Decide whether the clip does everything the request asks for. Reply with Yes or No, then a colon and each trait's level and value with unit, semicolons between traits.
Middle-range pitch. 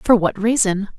No: high, 205 Hz